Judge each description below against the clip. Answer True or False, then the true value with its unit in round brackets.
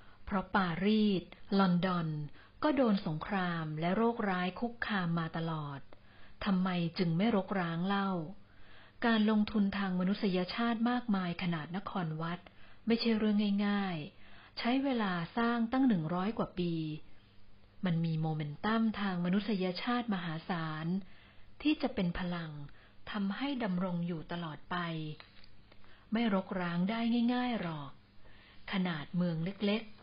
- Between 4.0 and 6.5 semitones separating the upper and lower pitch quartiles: True (4.7 semitones)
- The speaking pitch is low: False (185 Hz)